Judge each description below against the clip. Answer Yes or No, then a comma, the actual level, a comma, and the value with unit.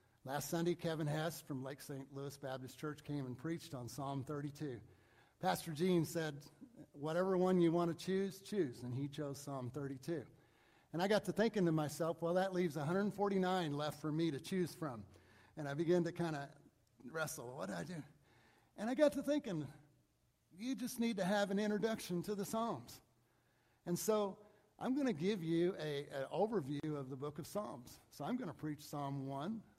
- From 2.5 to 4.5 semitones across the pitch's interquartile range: No, average, 5.1 semitones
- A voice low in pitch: No, medium, 160 Hz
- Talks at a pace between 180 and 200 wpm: Yes, average, 190 wpm